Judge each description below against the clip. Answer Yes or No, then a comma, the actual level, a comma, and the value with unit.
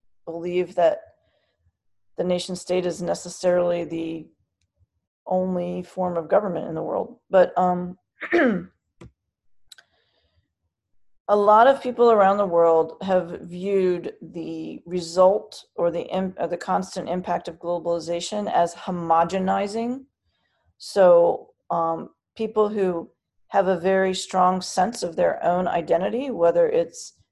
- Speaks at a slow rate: Yes, slow, 115 wpm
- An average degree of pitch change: No, narrow, 2.3 semitones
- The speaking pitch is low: No, medium, 180 Hz